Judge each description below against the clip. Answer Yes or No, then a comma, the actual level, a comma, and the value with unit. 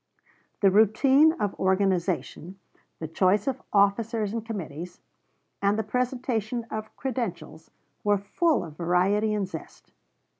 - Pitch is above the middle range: Yes, high, 205 Hz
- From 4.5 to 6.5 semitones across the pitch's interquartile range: No, average, 3.7 semitones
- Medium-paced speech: No, slow, 120 wpm